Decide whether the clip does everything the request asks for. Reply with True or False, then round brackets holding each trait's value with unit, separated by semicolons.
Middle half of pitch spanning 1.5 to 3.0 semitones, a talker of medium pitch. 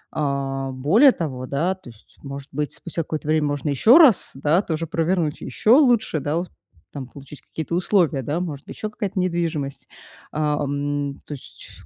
False (4.0 semitones; 150 Hz)